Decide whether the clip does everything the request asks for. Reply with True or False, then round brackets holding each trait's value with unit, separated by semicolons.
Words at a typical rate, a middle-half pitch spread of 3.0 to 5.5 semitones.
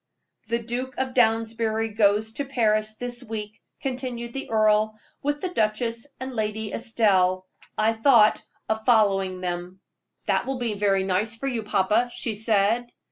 False (150 wpm; 2.4 semitones)